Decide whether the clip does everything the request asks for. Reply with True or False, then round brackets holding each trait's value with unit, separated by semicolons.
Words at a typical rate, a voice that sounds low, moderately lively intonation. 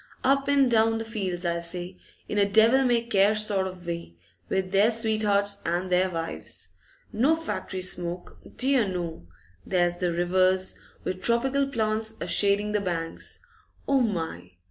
False (155 wpm; 200 Hz; 4.1 semitones)